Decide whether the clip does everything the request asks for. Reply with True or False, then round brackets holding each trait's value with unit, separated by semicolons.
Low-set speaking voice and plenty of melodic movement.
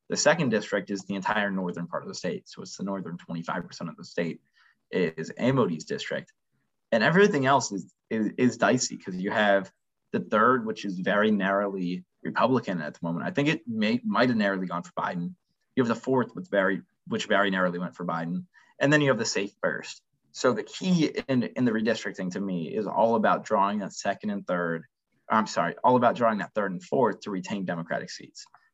True (100 Hz; 6.3 semitones)